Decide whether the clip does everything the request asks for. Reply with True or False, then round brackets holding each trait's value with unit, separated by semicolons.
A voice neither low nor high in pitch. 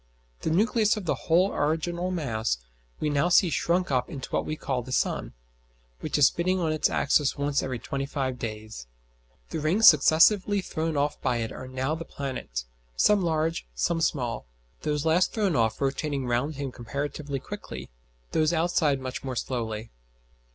True (145 Hz)